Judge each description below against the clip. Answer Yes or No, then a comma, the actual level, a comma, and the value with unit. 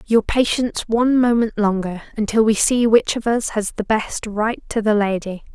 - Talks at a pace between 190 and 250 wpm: Yes, average, 195 wpm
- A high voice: Yes, high, 220 Hz